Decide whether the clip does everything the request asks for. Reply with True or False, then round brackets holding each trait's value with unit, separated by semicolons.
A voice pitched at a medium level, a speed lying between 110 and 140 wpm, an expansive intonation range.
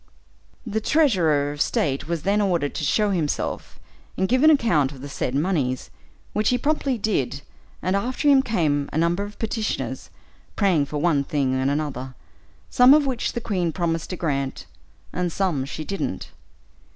False (170 Hz; 170 wpm; 6.9 semitones)